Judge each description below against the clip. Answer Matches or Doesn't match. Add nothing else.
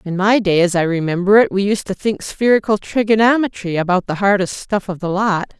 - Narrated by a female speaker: Matches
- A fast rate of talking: Matches